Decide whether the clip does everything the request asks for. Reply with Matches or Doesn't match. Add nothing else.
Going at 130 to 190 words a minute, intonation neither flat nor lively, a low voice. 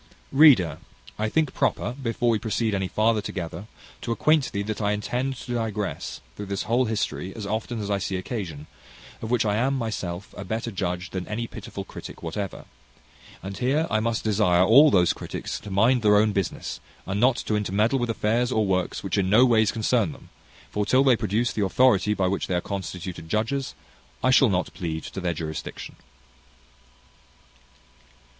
Matches